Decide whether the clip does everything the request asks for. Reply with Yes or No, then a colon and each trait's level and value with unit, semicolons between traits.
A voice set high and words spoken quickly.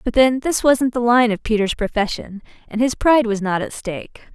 Yes: high, 230 Hz; fast, 220 wpm